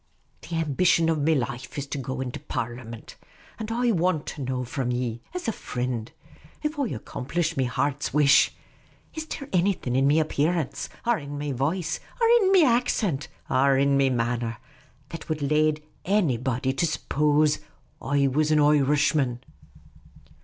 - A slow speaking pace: No, average, 165 wpm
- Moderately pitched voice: Yes, medium, 145 Hz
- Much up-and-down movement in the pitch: No, average, 4.1 semitones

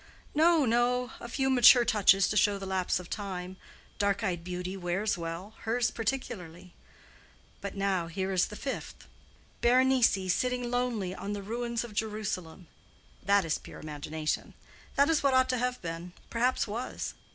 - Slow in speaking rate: No, average, 155 wpm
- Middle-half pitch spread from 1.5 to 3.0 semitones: No, average, 5.1 semitones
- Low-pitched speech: No, high, 205 Hz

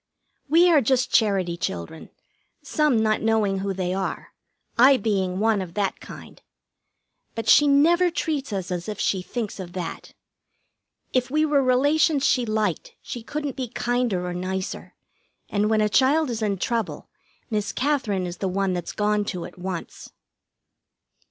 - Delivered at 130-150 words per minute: No, average, 160 wpm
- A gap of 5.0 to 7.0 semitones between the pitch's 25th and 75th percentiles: Yes, wide, 5.6 semitones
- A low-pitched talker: No, high, 215 Hz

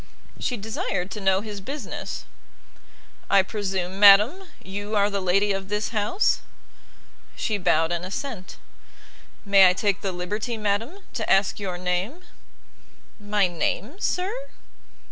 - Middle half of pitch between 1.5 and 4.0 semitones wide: Yes, narrow, 2.4 semitones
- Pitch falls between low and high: No, high, 200 Hz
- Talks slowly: Yes, slow, 130 wpm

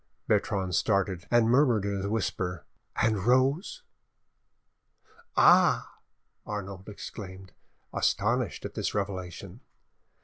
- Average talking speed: No, slow, 95 wpm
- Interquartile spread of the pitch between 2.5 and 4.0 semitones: Yes, average, 3.1 semitones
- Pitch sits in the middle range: No, low, 100 Hz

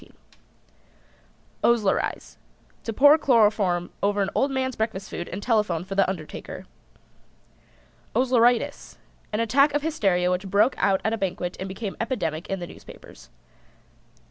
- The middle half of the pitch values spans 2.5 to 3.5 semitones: No, average, 4.2 semitones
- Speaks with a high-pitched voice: Yes, high, 205 Hz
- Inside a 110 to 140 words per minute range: Yes, slow, 135 wpm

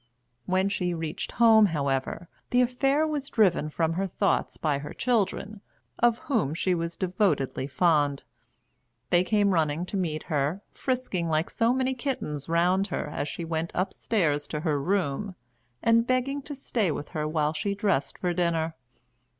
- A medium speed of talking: Yes, average, 160 wpm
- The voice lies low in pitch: No, medium, 180 Hz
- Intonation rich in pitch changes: Yes, wide, 6.1 semitones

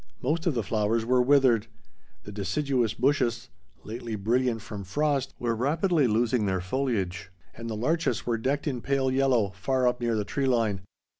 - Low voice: Yes, low, 120 Hz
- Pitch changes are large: No, average, 3.8 semitones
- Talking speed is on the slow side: No, average, 170 wpm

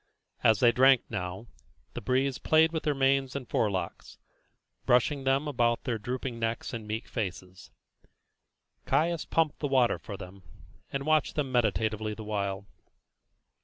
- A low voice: Yes, low, 120 Hz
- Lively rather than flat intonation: No, average, 4.3 semitones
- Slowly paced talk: No, average, 145 wpm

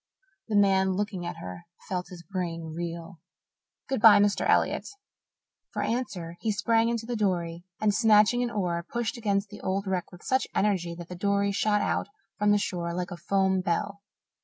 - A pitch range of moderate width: Yes, average, 3.1 semitones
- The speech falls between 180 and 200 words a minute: Yes, average, 185 wpm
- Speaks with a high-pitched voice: Yes, high, 195 Hz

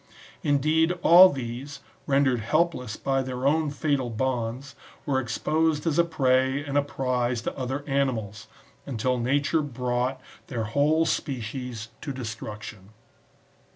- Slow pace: Yes, slow, 125 wpm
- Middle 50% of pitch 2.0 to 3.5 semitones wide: Yes, average, 2.9 semitones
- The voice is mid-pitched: No, low, 130 Hz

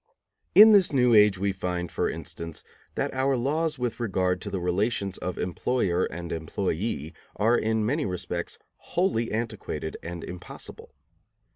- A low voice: Yes, low, 105 Hz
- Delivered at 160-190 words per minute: No, average, 145 wpm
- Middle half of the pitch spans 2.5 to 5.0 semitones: No, wide, 5.6 semitones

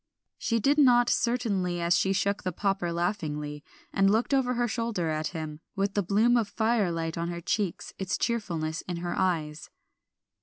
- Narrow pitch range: No, average, 5.2 semitones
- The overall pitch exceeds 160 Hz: Yes, high, 190 Hz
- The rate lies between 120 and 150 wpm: No, average, 180 wpm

